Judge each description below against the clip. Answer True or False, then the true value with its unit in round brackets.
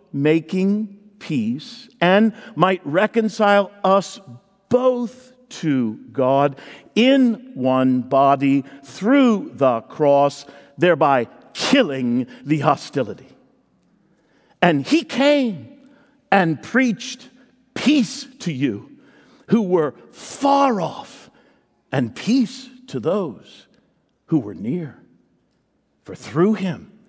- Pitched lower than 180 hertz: False (200 Hz)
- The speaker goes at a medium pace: False (90 wpm)